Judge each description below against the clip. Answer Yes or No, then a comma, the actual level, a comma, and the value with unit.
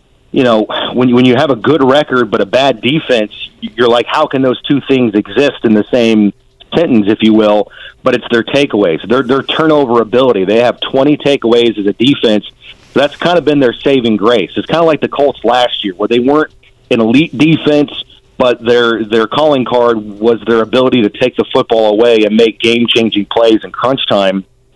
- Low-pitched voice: Yes, low, 120 Hz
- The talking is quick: Yes, fast, 210 wpm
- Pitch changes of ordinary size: Yes, average, 3.3 semitones